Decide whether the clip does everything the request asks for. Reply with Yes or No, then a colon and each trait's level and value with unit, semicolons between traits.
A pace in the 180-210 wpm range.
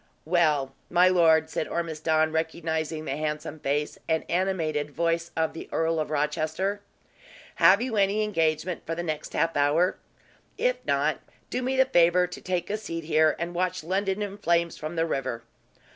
No: average, 170 wpm